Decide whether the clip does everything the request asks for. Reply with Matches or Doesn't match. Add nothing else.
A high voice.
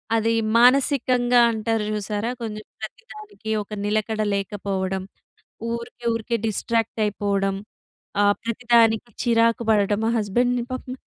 Matches